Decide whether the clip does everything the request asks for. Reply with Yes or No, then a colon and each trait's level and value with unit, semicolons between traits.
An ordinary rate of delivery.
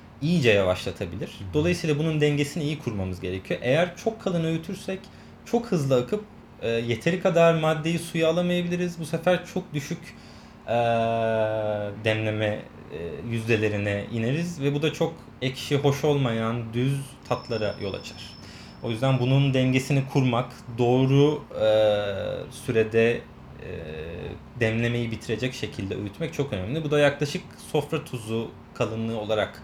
Yes: average, 130 wpm